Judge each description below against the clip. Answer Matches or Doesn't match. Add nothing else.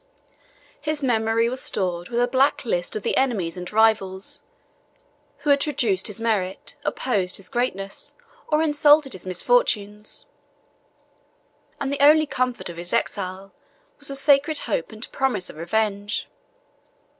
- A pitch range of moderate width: Doesn't match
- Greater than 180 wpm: Doesn't match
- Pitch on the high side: Matches